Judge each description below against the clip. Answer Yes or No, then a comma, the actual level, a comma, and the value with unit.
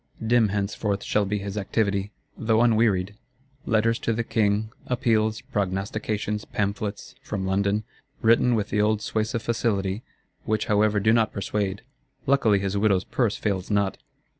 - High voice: No, low, 105 Hz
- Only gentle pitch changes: Yes, narrow, 1.8 semitones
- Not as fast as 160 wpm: Yes, average, 140 wpm